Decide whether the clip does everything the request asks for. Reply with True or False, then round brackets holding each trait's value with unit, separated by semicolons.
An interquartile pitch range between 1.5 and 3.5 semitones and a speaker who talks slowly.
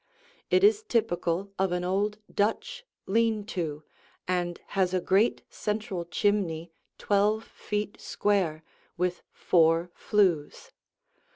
True (3.2 semitones; 110 wpm)